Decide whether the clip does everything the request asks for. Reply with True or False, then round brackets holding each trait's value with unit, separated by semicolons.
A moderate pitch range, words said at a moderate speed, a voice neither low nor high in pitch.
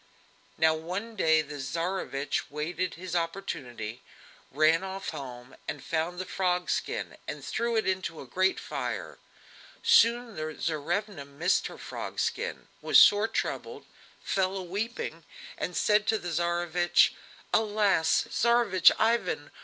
False (4.3 semitones; 130 wpm; 180 Hz)